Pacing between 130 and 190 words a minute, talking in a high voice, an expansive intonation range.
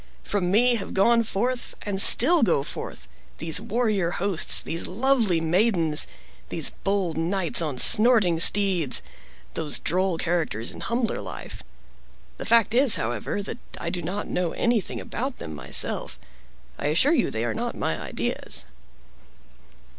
Yes: average, 145 wpm; high, 195 Hz; wide, 5.8 semitones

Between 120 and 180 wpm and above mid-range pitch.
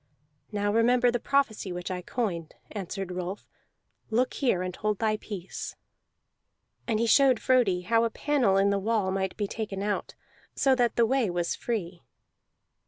Yes: average, 165 wpm; high, 210 Hz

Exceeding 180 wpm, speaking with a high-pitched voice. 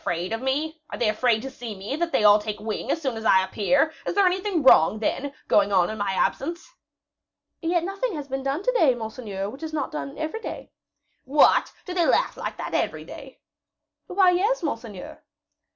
Yes: average, 195 wpm; very high, 270 Hz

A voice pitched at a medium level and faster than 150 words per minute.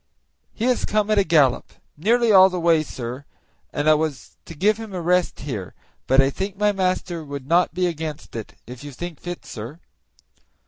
Yes: medium, 165 Hz; average, 195 wpm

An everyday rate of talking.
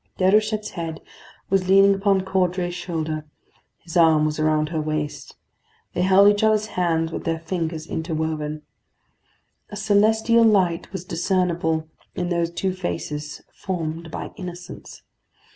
No: slow, 130 wpm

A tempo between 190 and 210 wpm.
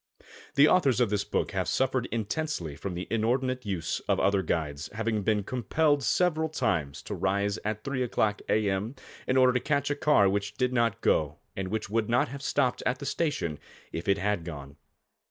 Yes: average, 195 wpm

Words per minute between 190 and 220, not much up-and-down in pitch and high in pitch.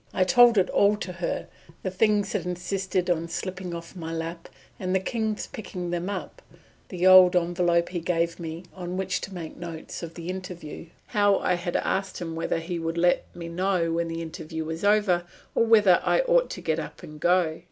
No: fast, 205 wpm; narrow, 2.2 semitones; medium, 180 Hz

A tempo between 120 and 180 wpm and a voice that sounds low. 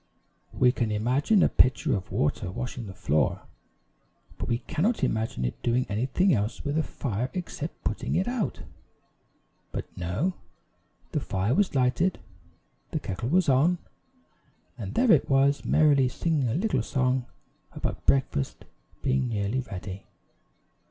Yes: average, 140 wpm; low, 130 Hz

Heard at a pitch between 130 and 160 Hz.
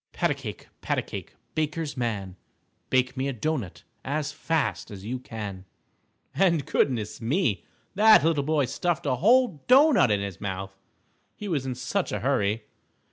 Yes: low, 135 Hz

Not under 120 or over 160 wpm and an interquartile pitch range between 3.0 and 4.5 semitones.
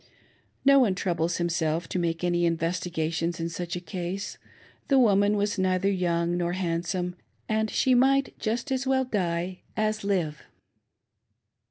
Yes: average, 150 wpm; average, 3.7 semitones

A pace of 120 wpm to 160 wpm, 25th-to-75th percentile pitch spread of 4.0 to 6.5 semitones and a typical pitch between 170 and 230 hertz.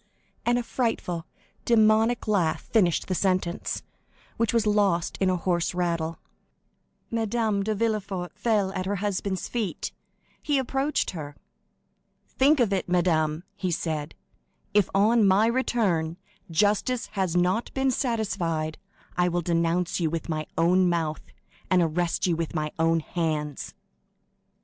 Yes: slow, 135 wpm; average, 4.5 semitones; medium, 185 Hz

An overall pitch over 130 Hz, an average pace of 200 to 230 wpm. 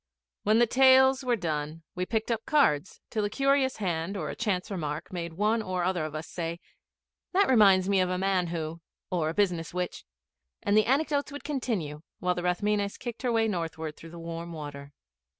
Yes: medium, 185 Hz; fast, 205 wpm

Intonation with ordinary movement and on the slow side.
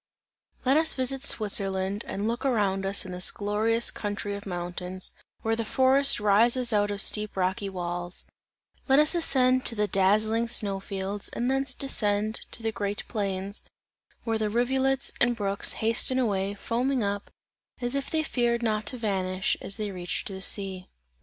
No: average, 3.7 semitones; average, 165 wpm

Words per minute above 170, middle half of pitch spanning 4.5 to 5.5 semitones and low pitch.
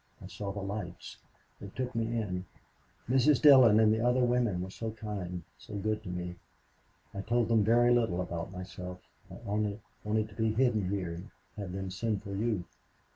No: average, 185 wpm; average, 3.5 semitones; low, 105 Hz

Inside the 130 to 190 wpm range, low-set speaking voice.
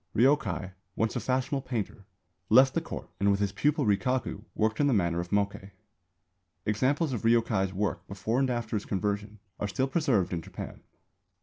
Yes: average, 175 wpm; low, 110 Hz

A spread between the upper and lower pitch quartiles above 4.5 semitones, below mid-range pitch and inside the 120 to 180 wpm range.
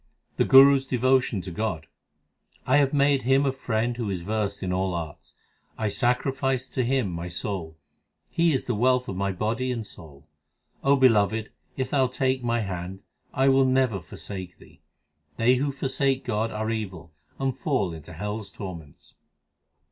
Yes: wide, 5.6 semitones; low, 115 Hz; average, 175 wpm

